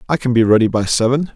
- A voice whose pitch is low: Yes, low, 120 Hz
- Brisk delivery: Yes, fast, 265 wpm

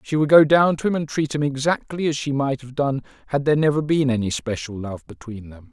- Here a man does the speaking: Yes, male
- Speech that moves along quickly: Yes, fast, 250 wpm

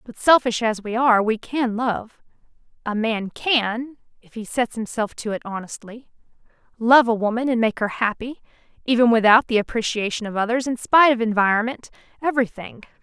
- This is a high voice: Yes, high, 230 Hz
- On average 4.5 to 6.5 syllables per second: Yes, 5.5 syllables/s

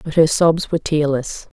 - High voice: No, medium, 160 Hz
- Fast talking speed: No, average, 190 wpm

